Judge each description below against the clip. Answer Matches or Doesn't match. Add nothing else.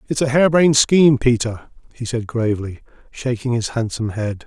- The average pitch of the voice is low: Matches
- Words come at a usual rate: Matches